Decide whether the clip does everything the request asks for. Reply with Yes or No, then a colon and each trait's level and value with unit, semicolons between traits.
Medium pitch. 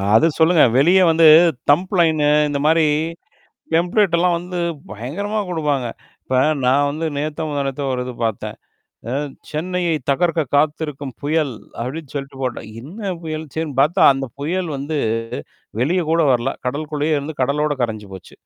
Yes: medium, 155 Hz